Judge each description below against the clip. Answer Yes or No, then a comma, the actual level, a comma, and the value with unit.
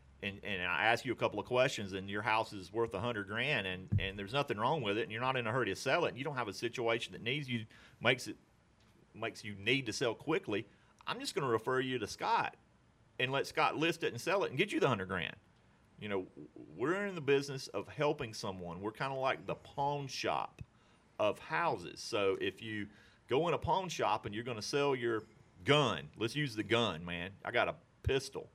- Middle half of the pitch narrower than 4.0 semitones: No, average, 4.7 semitones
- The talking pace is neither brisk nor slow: No, fast, 240 wpm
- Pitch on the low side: Yes, low, 115 Hz